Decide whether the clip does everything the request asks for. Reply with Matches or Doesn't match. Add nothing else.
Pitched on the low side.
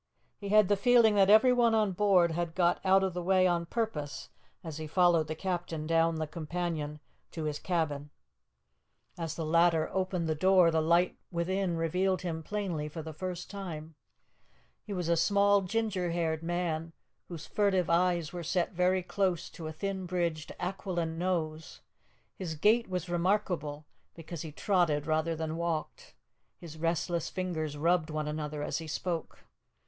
Doesn't match